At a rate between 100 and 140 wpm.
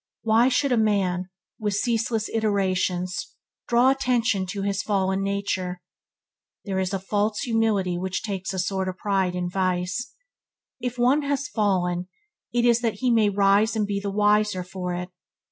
No: average, 160 wpm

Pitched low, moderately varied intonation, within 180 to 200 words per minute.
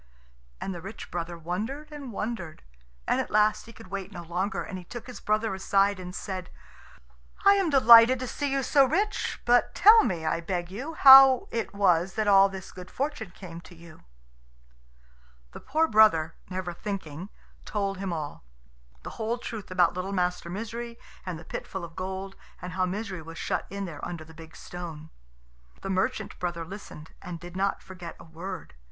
No: high, 190 Hz; average, 4.4 semitones; average, 185 wpm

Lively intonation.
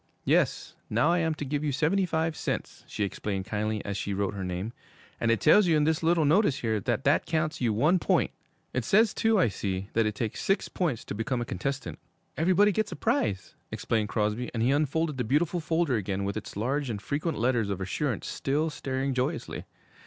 Yes: wide, 7.0 semitones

